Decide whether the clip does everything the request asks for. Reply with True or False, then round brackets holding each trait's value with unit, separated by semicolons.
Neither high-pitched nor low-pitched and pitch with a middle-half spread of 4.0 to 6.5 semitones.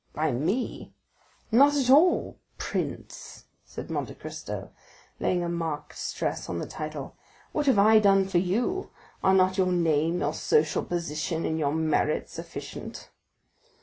True (175 Hz; 4.8 semitones)